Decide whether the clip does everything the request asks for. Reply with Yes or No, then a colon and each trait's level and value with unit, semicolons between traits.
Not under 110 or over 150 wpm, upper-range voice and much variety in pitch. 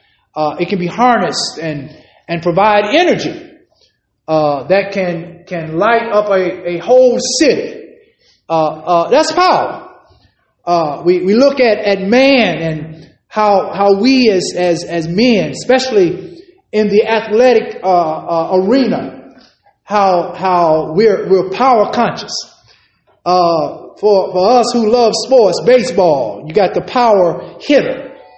Yes: slow, 135 wpm; high, 200 Hz; wide, 6.0 semitones